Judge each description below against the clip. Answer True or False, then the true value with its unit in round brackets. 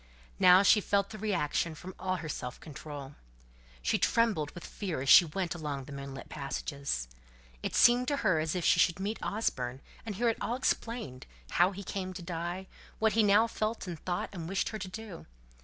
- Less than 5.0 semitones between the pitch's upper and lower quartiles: False (5.6 semitones)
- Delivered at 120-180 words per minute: False (200 wpm)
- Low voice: False (180 Hz)